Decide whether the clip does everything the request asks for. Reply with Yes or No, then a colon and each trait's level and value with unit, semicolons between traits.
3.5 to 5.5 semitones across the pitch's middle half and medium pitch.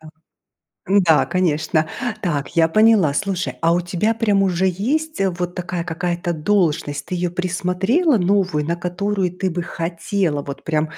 No: average, 2.9 semitones; medium, 180 Hz